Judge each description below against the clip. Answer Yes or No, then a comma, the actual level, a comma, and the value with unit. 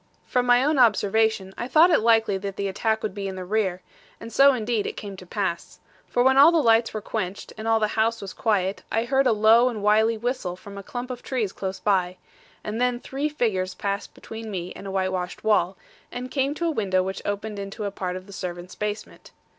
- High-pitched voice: Yes, high, 215 Hz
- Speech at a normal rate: No, fast, 230 wpm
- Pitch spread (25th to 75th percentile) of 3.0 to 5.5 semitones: Yes, average, 3.9 semitones